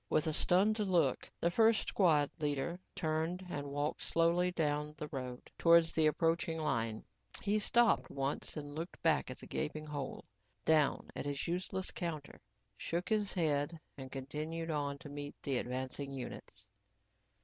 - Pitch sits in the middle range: Yes, medium, 155 Hz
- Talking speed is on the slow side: No, average, 155 wpm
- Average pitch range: Yes, average, 3.0 semitones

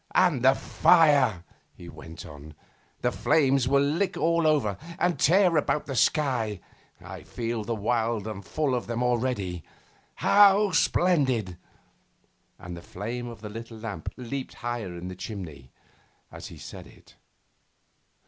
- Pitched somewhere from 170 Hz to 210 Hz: No, low, 120 Hz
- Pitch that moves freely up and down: Yes, wide, 6.3 semitones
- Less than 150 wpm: Yes, average, 140 wpm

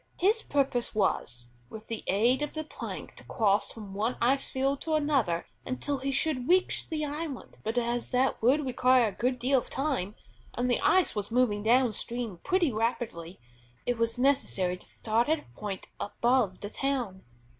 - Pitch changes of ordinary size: Yes, average, 4.2 semitones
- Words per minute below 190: Yes, average, 180 wpm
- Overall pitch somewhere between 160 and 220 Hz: No, high, 245 Hz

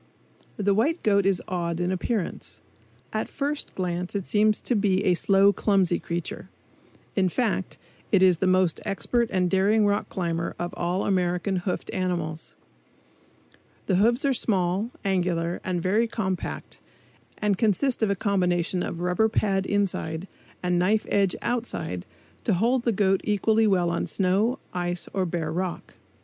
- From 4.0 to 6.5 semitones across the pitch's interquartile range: No, average, 3.0 semitones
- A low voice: No, high, 190 Hz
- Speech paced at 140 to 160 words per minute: Yes, average, 155 wpm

